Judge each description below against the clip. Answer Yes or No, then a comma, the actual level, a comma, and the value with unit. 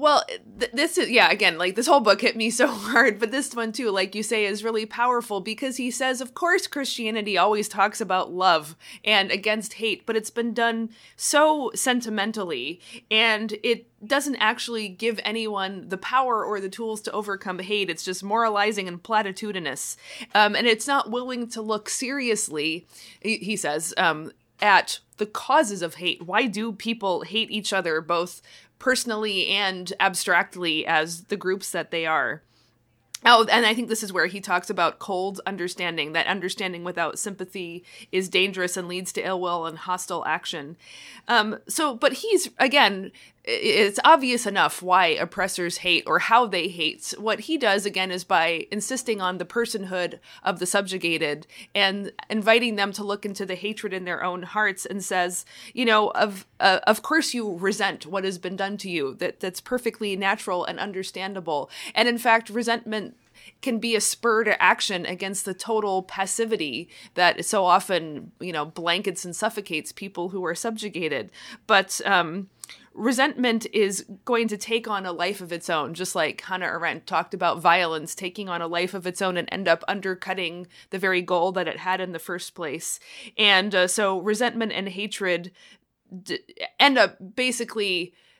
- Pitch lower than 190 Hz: No, high, 200 Hz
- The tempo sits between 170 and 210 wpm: Yes, average, 175 wpm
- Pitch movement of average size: Yes, average, 3.8 semitones